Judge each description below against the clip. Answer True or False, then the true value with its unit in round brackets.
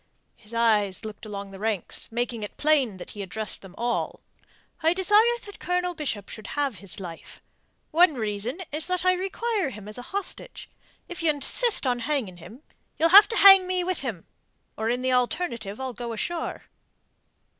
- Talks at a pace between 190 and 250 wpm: False (180 wpm)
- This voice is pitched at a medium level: False (250 Hz)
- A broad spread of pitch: True (8.9 semitones)